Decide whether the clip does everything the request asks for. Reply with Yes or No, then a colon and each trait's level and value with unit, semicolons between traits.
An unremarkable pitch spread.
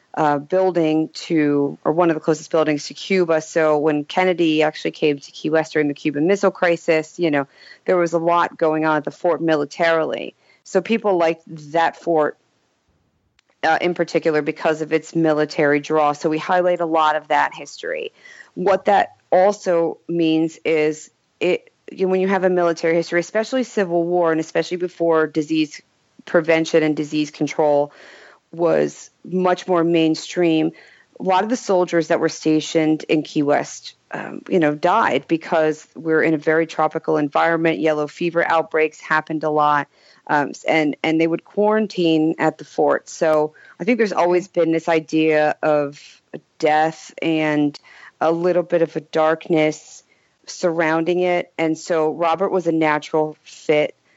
No: narrow, 1.8 semitones